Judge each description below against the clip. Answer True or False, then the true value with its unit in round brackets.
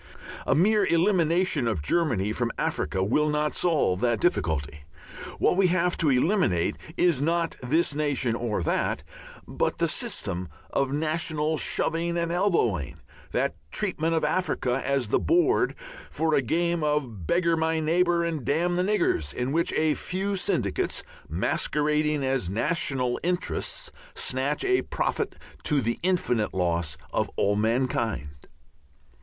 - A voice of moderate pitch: True (150 Hz)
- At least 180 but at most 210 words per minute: False (140 wpm)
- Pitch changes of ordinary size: False (6.1 semitones)